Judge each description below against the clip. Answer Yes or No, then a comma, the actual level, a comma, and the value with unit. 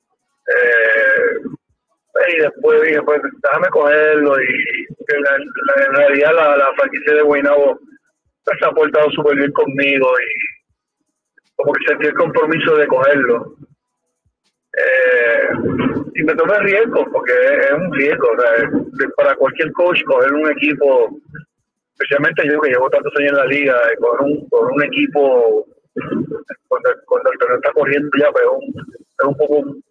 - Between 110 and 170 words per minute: Yes, average, 155 wpm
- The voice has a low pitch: No, very high, 275 Hz